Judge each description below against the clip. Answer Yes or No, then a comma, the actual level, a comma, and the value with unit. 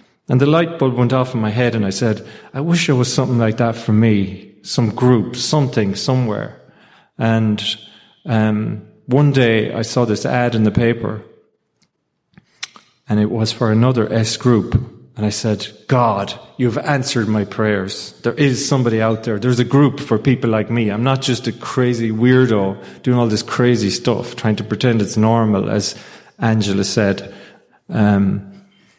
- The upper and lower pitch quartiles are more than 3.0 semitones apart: No, average, 2.7 semitones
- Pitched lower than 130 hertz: Yes, low, 115 Hz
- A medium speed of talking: Yes, average, 170 wpm